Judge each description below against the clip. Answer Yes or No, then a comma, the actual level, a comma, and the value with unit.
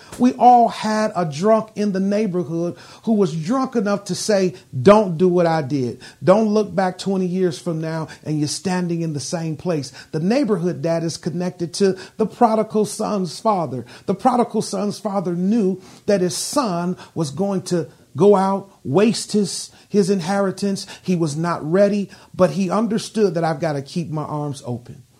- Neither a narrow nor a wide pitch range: Yes, average, 3.7 semitones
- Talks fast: No, average, 180 wpm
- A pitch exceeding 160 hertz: Yes, medium, 185 Hz